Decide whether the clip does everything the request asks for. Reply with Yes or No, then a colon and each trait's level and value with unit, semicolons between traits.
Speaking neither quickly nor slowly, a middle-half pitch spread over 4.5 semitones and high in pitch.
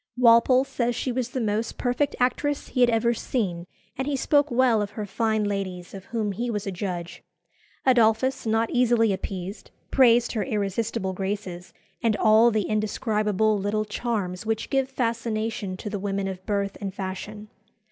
No: average, 165 wpm; average, 3.2 semitones; high, 215 Hz